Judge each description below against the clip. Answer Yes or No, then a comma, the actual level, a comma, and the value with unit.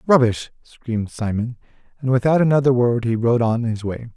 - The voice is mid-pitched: No, low, 120 Hz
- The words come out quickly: No, average, 175 wpm